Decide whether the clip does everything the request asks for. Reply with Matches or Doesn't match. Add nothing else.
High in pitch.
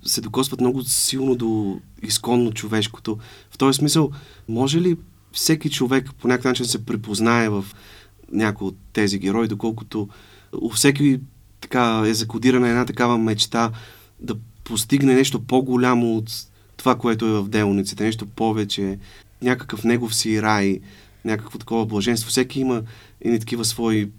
Doesn't match